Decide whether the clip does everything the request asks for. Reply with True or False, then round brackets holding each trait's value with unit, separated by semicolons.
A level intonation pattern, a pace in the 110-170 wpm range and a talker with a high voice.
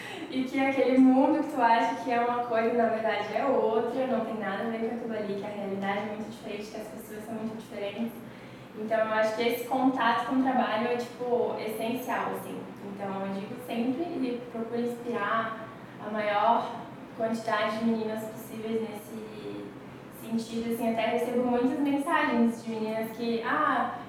False (1.6 semitones; 180 wpm; 230 Hz)